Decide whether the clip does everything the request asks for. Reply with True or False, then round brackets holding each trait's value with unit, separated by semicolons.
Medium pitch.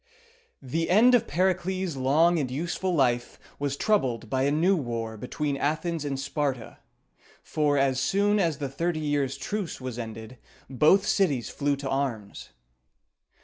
True (145 Hz)